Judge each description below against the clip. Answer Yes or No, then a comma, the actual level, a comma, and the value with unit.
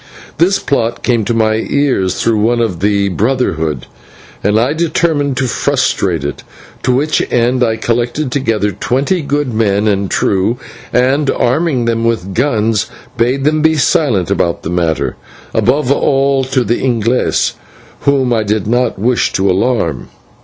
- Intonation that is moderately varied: Yes, average, 4.5 semitones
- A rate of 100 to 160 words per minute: Yes, average, 155 wpm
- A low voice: Yes, low, 120 Hz